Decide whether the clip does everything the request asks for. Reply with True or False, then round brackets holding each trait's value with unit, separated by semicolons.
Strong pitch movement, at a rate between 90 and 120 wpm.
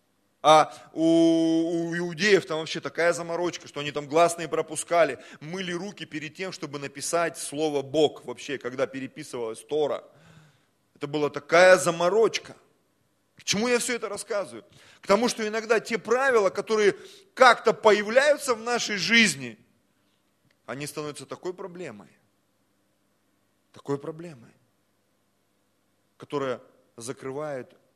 True (6.5 semitones; 115 wpm)